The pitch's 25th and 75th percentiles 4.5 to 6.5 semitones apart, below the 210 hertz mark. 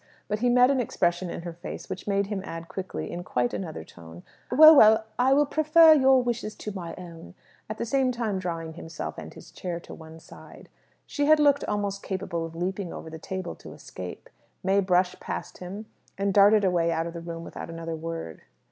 Yes: average, 4.8 semitones; high, 190 Hz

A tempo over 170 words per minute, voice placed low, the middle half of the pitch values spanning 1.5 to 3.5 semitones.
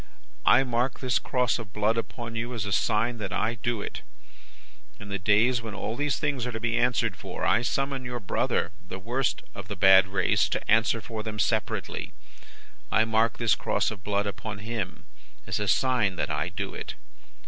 Yes: average, 195 wpm; low, 115 Hz; average, 2.9 semitones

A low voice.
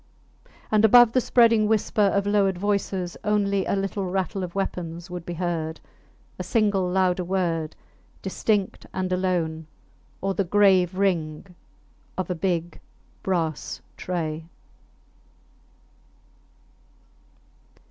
No: medium, 185 Hz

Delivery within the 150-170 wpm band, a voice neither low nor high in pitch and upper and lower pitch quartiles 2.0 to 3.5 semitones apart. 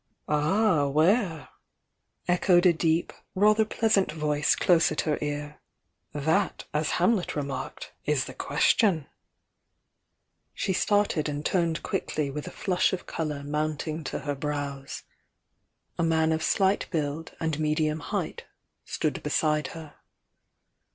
No: average, 140 wpm; medium, 160 Hz; average, 3.1 semitones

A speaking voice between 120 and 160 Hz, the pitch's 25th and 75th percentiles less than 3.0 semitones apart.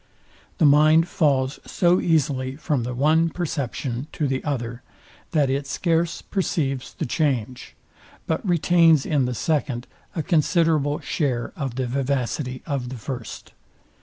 No: medium, 140 Hz; average, 3.7 semitones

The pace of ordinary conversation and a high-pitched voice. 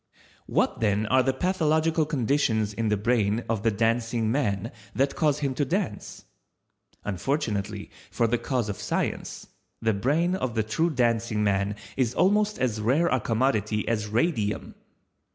No: average, 150 wpm; low, 115 Hz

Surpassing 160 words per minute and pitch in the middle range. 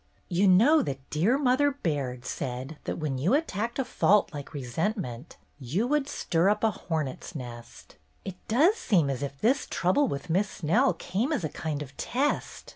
Yes: average, 185 wpm; medium, 180 Hz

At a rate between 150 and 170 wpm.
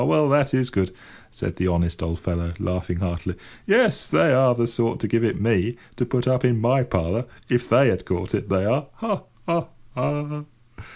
No: average, 195 wpm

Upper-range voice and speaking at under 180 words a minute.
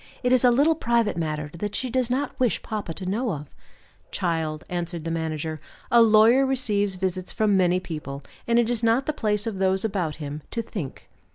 No: high, 200 Hz; average, 200 wpm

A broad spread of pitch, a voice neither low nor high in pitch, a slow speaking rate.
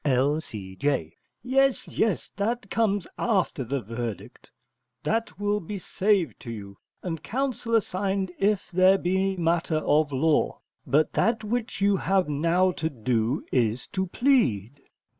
Yes: wide, 6.9 semitones; medium, 180 Hz; slow, 130 wpm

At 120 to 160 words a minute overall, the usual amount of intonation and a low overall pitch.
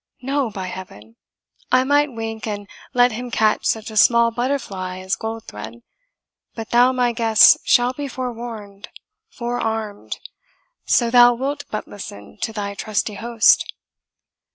No: slow, 135 wpm; average, 3.1 semitones; high, 225 Hz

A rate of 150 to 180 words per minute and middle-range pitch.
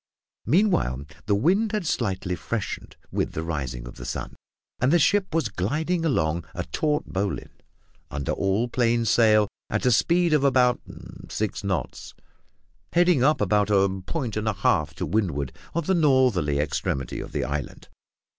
No: average, 165 wpm; low, 110 Hz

